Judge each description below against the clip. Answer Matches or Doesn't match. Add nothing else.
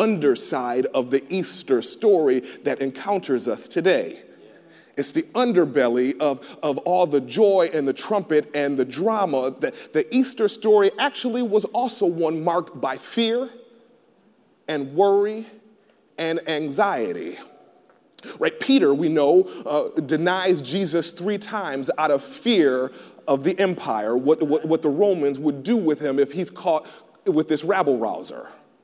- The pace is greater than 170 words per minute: Doesn't match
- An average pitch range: Doesn't match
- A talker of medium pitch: Matches